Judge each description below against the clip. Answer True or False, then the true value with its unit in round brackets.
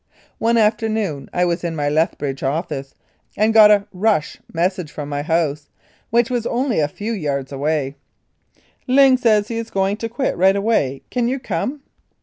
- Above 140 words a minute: True (180 wpm)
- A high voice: True (195 Hz)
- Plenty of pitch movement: True (7.2 semitones)